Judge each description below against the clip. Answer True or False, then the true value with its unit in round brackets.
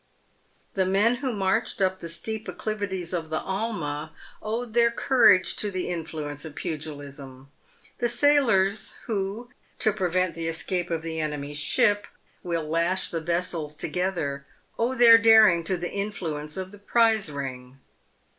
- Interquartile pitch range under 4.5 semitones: False (5.3 semitones)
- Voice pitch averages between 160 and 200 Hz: True (185 Hz)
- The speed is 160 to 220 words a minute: False (150 wpm)